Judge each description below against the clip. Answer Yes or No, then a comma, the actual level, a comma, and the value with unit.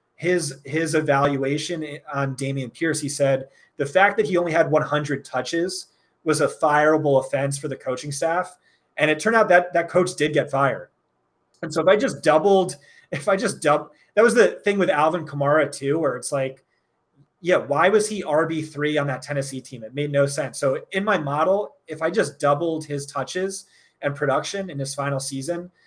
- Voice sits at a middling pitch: Yes, medium, 150 Hz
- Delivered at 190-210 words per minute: Yes, average, 195 wpm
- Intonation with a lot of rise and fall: No, average, 3.9 semitones